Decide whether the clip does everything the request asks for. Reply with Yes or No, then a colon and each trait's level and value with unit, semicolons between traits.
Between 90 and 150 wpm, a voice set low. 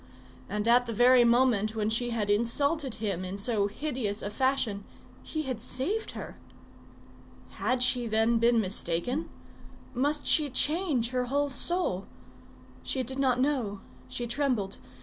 No: average, 145 wpm; high, 245 Hz